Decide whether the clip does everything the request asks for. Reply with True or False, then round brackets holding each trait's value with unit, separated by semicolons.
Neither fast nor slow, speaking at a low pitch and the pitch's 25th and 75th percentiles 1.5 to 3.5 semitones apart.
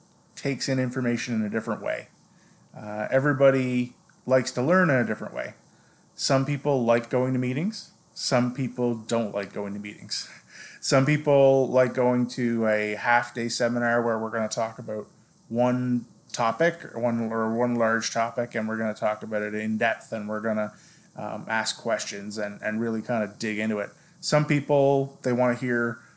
True (185 wpm; 120 Hz; 2.7 semitones)